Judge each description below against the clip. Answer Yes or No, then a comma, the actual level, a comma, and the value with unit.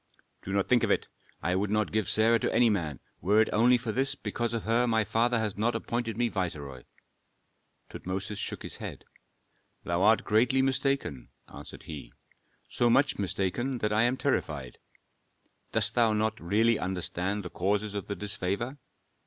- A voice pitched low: Yes, low, 110 Hz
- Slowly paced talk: No, average, 175 wpm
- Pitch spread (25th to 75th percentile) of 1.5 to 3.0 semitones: No, average, 3.7 semitones